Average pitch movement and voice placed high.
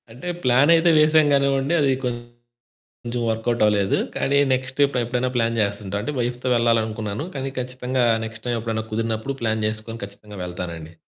No: average, 3.1 semitones; low, 120 Hz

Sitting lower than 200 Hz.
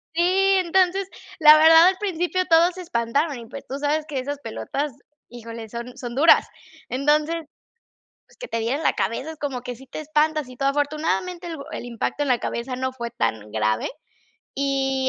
No: very high, 280 Hz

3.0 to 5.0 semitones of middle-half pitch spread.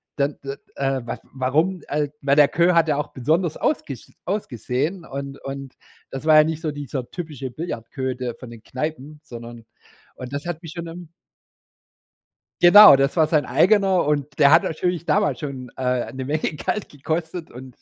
Yes: average, 4.0 semitones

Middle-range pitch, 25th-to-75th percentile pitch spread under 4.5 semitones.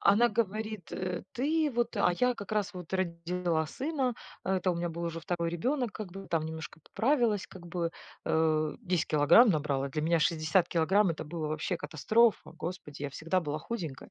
No: medium, 180 Hz; average, 5.0 semitones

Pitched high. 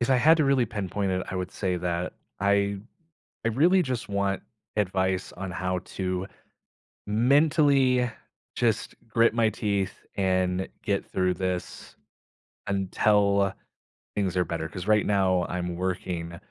No: low, 100 Hz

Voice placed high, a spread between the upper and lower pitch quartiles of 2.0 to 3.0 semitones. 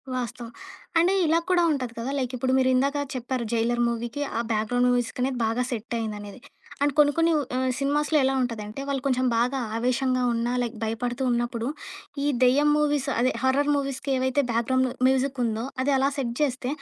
Yes: very high, 255 Hz; average, 2.7 semitones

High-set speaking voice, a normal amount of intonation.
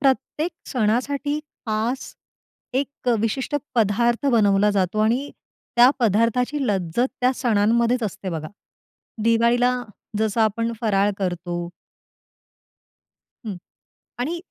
Yes: high, 230 Hz; average, 3.4 semitones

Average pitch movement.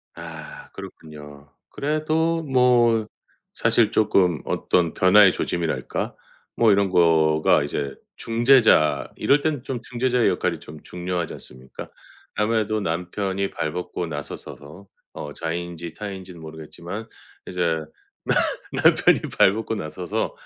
No: wide, 6.0 semitones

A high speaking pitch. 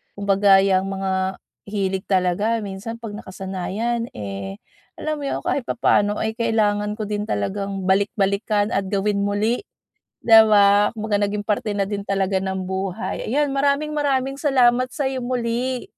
Yes: high, 205 Hz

